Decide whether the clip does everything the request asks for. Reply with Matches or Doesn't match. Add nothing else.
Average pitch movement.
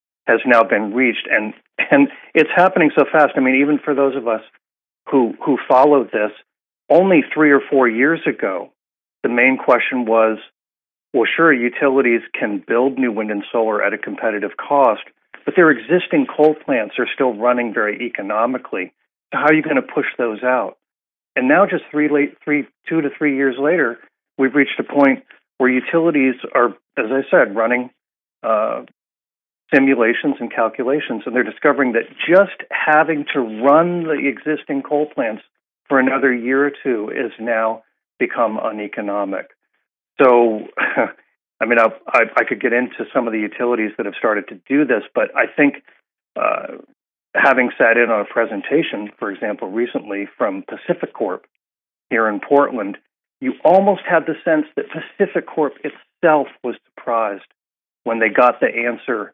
Matches